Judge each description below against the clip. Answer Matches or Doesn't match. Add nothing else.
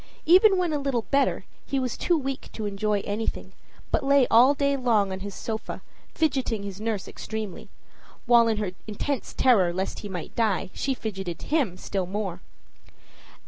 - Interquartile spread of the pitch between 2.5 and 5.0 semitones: Doesn't match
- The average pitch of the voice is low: Doesn't match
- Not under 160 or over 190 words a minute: Matches